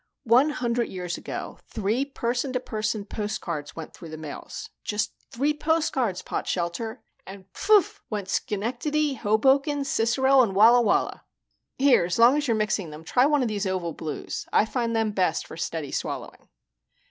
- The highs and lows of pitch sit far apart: Yes, wide, 5.7 semitones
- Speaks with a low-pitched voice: No, high, 225 Hz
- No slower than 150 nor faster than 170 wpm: Yes, average, 160 wpm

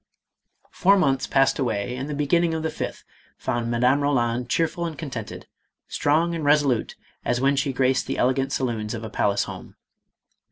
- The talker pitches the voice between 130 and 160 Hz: Yes, low, 135 Hz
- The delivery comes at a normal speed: Yes, average, 170 wpm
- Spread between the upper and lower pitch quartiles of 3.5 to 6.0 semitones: Yes, average, 3.8 semitones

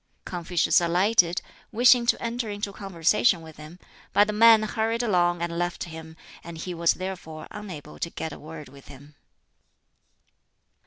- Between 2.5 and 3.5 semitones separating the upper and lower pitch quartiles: No, average, 4.5 semitones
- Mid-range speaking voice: Yes, medium, 175 Hz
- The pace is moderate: Yes, average, 155 wpm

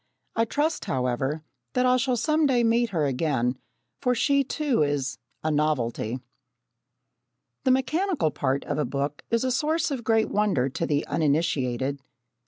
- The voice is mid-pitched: Yes, medium, 160 Hz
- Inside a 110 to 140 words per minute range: No, average, 155 wpm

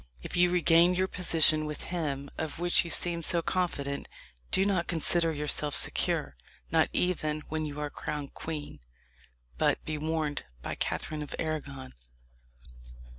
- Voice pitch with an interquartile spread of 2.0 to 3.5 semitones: Yes, narrow, 2.6 semitones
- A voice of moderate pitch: Yes, medium, 155 Hz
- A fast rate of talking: No, average, 145 wpm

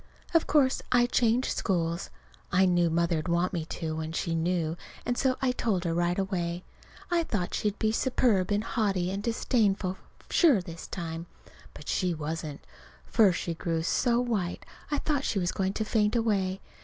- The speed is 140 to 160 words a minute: No, average, 175 wpm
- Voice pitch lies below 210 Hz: Yes, high, 190 Hz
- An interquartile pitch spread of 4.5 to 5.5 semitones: Yes, average, 4.9 semitones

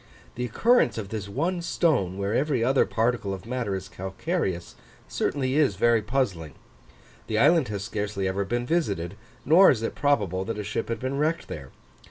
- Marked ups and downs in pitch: Yes, wide, 5.9 semitones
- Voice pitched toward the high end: No, low, 115 Hz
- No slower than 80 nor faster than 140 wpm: No, average, 180 wpm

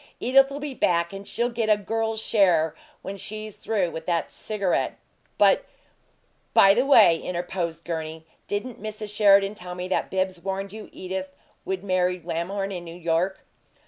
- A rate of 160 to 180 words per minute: Yes, average, 165 wpm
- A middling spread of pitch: Yes, average, 3.3 semitones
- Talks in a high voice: Yes, high, 195 Hz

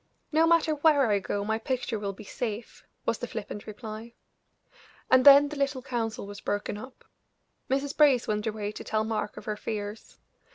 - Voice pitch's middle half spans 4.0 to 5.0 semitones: Yes, average, 4.6 semitones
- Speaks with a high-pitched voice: Yes, high, 225 Hz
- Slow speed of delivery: No, average, 180 wpm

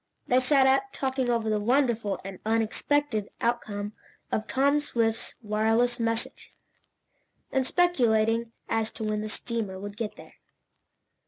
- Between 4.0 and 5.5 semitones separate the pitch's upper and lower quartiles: No, average, 3.2 semitones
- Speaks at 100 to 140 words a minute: Yes, slow, 135 wpm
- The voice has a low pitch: No, high, 230 Hz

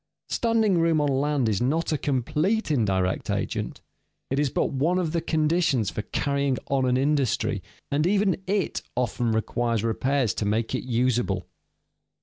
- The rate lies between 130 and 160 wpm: Yes, average, 155 wpm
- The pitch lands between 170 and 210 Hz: No, medium, 140 Hz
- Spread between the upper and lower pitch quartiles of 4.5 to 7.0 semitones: Yes, average, 5.2 semitones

